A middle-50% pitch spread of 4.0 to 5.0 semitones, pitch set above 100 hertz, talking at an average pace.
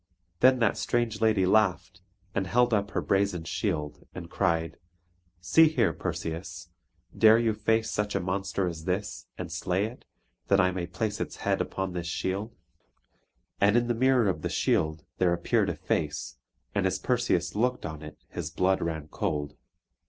No: average, 4.5 semitones; very low, 95 Hz; average, 170 wpm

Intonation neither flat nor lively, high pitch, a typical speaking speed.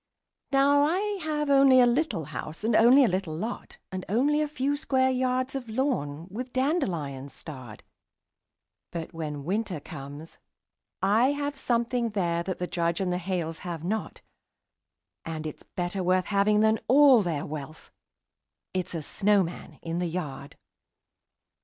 No: wide, 7.8 semitones; high, 195 Hz; average, 150 wpm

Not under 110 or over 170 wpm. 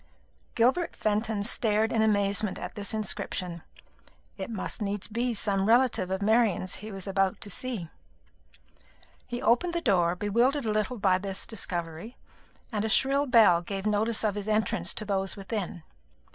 Yes: average, 160 wpm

